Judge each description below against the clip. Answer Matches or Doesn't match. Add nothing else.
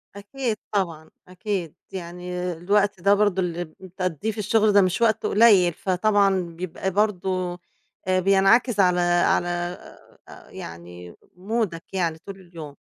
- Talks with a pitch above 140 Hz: Matches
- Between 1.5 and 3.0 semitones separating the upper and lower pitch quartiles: Matches